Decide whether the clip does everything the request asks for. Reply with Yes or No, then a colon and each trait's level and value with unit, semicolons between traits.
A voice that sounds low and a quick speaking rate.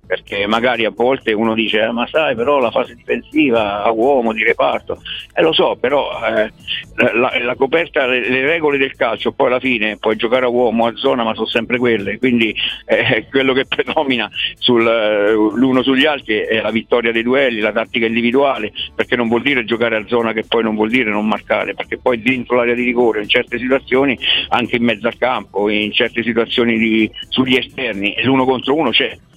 Yes: low, 120 Hz; fast, 200 wpm